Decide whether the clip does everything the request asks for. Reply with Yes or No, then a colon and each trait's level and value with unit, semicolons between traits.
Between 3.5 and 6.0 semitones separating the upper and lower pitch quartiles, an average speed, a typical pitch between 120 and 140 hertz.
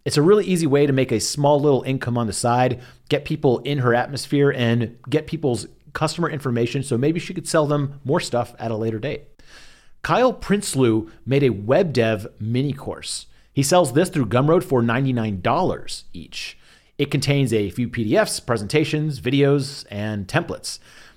Yes: average, 4.0 semitones; average, 175 wpm; low, 135 Hz